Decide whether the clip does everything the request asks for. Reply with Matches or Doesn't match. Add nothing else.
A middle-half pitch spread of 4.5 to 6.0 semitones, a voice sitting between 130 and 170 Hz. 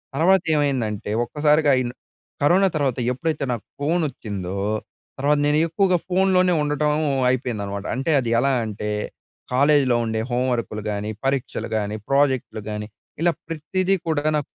Matches